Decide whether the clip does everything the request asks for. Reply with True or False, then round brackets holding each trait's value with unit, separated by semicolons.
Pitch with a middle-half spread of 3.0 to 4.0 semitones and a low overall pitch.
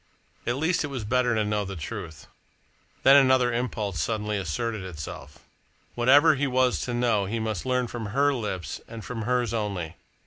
True (3.6 semitones; 115 Hz)